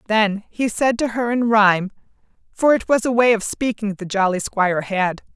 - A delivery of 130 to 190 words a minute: No, average, 200 wpm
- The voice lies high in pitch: Yes, high, 215 Hz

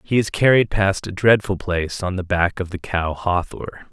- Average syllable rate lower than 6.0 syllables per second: Yes, 5.2 syllables/s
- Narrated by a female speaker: No, male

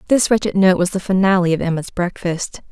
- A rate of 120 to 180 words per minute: No, average, 200 wpm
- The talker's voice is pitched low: No, medium, 185 Hz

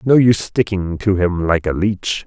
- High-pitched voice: No, low, 100 Hz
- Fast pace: Yes, fast, 210 wpm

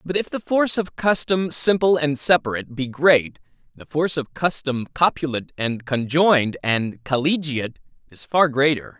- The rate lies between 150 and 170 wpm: Yes, average, 155 wpm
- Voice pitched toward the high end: No, medium, 150 Hz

